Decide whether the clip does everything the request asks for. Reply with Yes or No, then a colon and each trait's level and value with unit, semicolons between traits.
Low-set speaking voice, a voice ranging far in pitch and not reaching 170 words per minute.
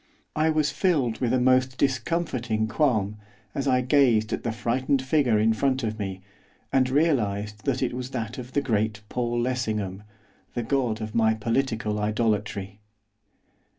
No: low, 120 Hz; average, 3.3 semitones; average, 155 wpm